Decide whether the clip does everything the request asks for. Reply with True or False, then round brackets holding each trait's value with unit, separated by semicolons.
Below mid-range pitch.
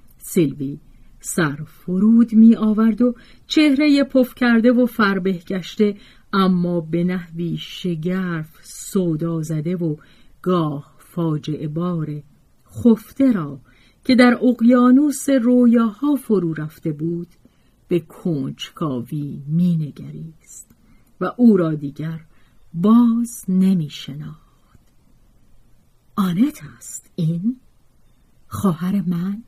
False (180 Hz)